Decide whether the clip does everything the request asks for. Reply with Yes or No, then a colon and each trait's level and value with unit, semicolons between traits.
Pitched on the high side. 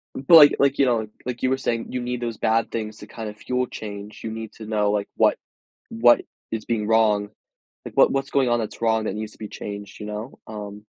No: low, 110 Hz